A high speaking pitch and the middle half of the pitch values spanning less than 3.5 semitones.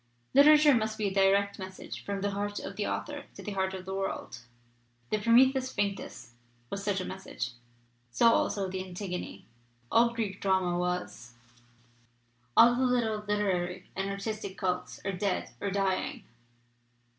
Yes: high, 200 Hz; narrow, 2.5 semitones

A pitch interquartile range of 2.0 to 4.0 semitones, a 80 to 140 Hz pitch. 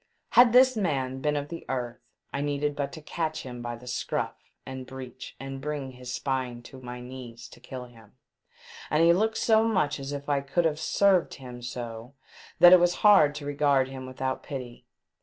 Yes: average, 3.3 semitones; low, 135 Hz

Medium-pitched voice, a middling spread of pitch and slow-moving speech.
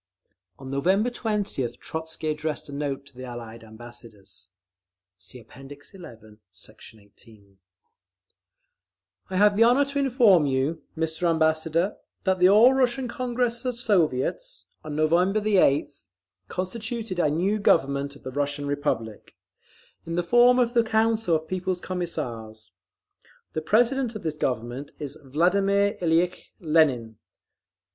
No: medium, 160 Hz; wide, 7.4 semitones; slow, 130 wpm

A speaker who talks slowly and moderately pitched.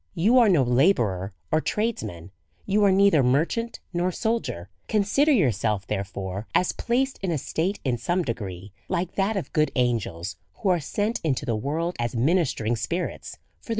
No: average, 170 wpm; medium, 155 Hz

